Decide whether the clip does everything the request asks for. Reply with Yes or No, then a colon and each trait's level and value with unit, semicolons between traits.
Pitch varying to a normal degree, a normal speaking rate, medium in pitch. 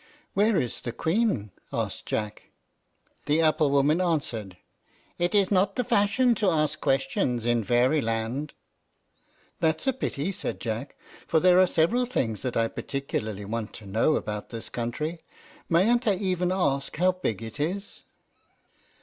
No: wide, 8.0 semitones; average, 145 wpm; medium, 150 Hz